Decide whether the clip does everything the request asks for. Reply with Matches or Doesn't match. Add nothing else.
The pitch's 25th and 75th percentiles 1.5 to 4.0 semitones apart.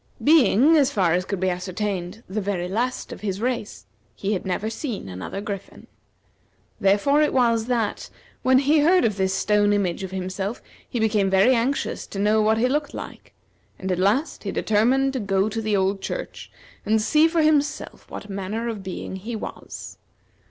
Doesn't match